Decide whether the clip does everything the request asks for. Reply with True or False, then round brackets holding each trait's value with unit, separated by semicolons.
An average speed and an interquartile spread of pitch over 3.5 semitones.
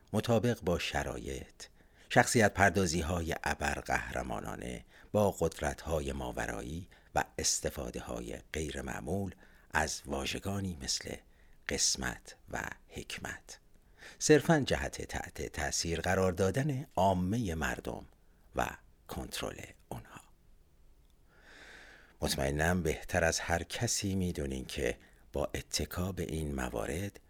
False (100 wpm; 5.3 semitones)